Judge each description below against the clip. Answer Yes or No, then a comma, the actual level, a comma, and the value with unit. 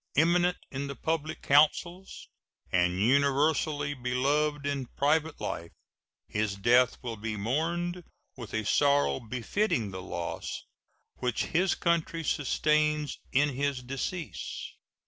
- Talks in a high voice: No, medium, 140 Hz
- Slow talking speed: Yes, slow, 115 wpm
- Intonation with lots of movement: No, average, 4.3 semitones